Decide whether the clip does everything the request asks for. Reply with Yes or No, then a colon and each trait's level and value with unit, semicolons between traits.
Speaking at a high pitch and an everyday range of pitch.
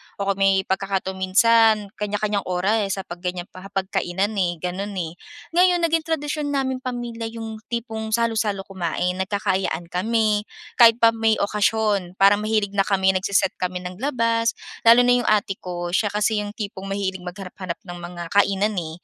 Yes: high, 200 Hz; average, 3.0 semitones